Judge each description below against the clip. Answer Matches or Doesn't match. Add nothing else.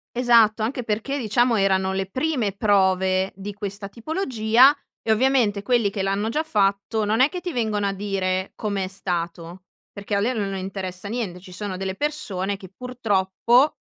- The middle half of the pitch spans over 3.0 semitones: Matches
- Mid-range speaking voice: Doesn't match